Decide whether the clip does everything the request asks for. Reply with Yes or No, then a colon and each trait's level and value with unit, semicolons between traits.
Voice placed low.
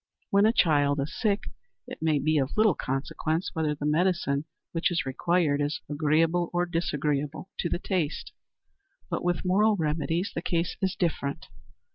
No: medium, 165 Hz